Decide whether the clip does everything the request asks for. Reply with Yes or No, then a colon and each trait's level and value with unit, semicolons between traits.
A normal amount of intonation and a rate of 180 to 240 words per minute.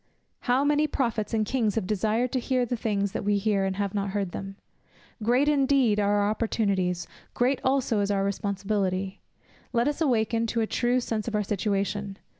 Yes: average, 3.5 semitones; average, 190 wpm